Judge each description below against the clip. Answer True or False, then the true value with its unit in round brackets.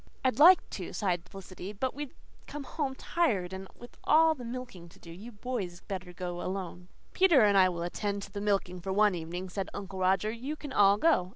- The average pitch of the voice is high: True (200 Hz)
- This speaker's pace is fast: True (210 wpm)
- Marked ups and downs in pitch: True (5.7 semitones)